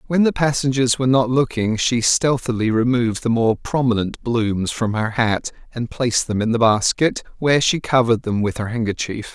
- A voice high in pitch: No, low, 120 Hz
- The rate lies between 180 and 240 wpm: Yes, average, 185 wpm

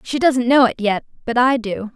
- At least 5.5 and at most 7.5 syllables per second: No, 5.0 syllables/s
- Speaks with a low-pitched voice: No, high, 240 Hz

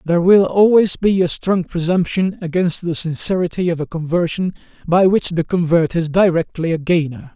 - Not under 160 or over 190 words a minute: Yes, average, 170 wpm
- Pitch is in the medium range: Yes, medium, 175 Hz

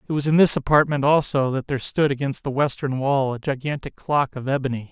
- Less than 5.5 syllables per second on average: No, 5.9 syllables/s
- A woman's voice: No, male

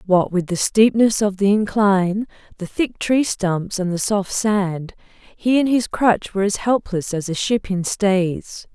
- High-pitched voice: Yes, high, 200 Hz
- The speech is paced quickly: No, average, 185 wpm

